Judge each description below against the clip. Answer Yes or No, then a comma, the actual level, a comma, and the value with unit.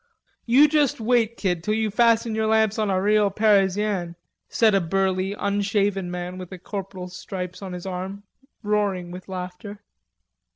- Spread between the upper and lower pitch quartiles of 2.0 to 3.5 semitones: Yes, narrow, 2.6 semitones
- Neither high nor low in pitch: No, high, 200 Hz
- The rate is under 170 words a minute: Yes, average, 160 wpm